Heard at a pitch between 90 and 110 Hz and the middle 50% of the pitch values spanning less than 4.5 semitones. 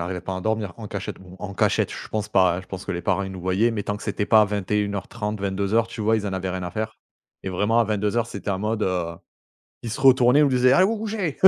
Yes: low, 105 Hz; average, 3.2 semitones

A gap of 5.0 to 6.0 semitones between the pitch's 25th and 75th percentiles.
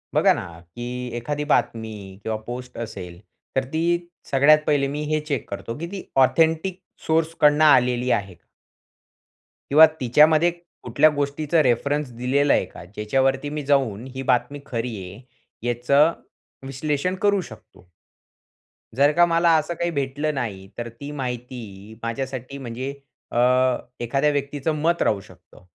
No: average, 4.2 semitones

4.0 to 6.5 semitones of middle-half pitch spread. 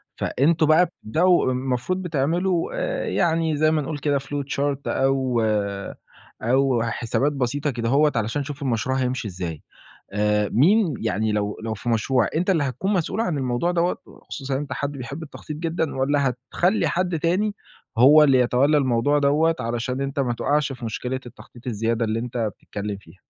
Yes: average, 4.6 semitones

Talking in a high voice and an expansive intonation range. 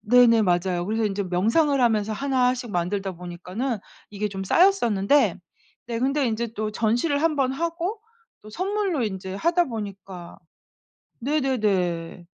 Yes: high, 225 Hz; wide, 6.1 semitones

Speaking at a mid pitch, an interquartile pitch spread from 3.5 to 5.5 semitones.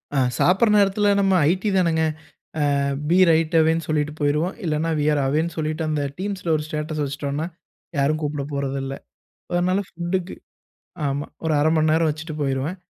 No: medium, 155 Hz; average, 2.8 semitones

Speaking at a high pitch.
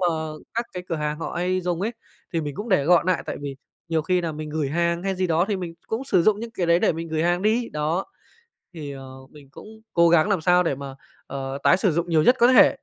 No: medium, 170 Hz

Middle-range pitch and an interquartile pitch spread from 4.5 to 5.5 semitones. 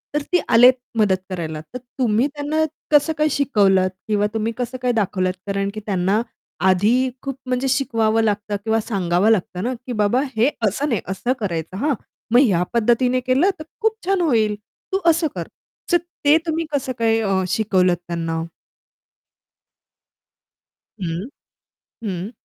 No: high, 225 Hz; average, 5.1 semitones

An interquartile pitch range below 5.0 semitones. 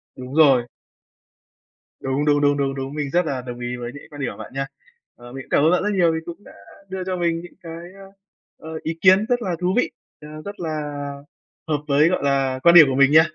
Yes: average, 4.3 semitones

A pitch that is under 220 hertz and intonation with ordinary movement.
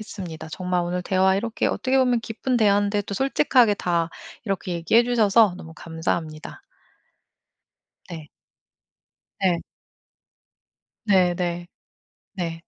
Yes: high, 190 Hz; average, 4.1 semitones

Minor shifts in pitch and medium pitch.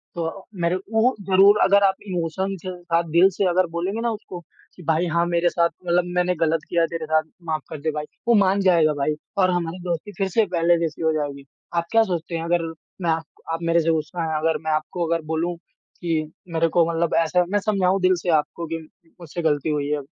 Yes: narrow, 2.3 semitones; medium, 170 Hz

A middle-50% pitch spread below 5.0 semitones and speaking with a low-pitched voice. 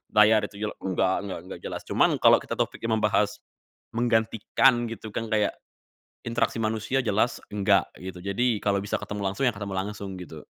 Yes: narrow, 2.5 semitones; low, 105 Hz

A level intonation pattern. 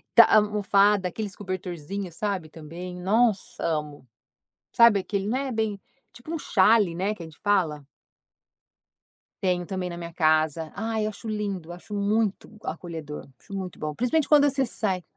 No: average, 3.9 semitones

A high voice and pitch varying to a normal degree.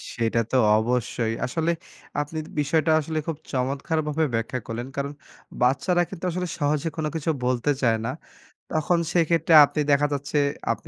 No: medium, 145 Hz; average, 4.1 semitones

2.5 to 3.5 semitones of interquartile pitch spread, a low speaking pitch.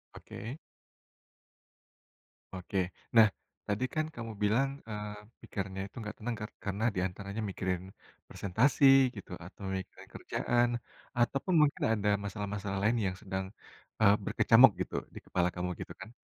Yes: average, 3.0 semitones; low, 105 Hz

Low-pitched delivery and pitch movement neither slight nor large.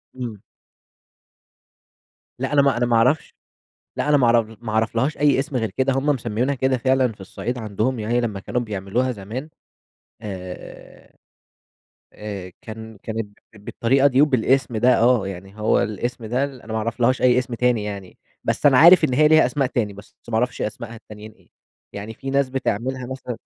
Yes: low, 120 Hz; average, 3.4 semitones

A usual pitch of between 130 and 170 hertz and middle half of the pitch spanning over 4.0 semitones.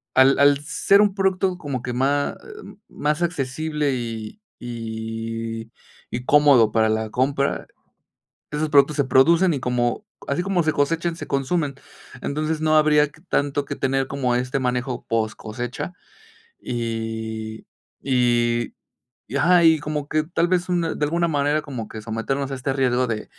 Yes: medium, 140 Hz; average, 4.4 semitones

